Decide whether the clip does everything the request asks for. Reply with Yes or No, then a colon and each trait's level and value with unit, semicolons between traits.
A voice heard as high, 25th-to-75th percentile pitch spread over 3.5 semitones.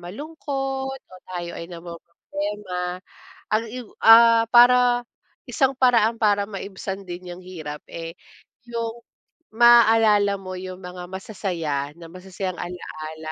Yes: high, 195 Hz; average, 4.6 semitones